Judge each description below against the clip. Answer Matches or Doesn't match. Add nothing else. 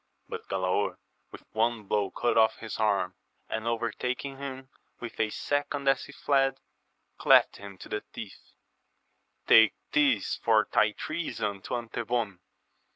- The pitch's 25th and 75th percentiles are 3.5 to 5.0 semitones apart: Matches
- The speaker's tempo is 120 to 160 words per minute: Matches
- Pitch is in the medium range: Doesn't match